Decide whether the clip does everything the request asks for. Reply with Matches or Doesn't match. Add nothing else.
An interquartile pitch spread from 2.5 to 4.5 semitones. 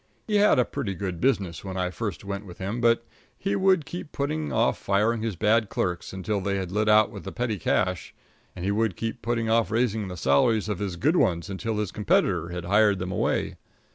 Matches